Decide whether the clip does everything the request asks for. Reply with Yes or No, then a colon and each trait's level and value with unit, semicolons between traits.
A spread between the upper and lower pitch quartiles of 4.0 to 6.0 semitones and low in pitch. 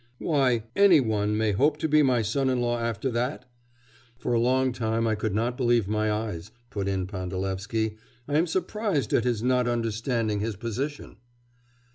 No: average, 3.4 semitones; low, 115 Hz